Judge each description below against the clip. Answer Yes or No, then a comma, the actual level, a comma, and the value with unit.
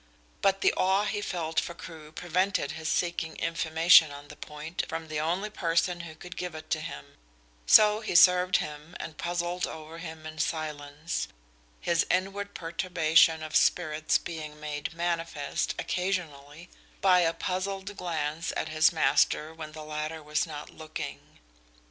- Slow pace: No, average, 155 wpm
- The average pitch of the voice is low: No, medium, 165 Hz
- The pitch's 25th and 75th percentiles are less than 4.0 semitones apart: Yes, narrow, 2.5 semitones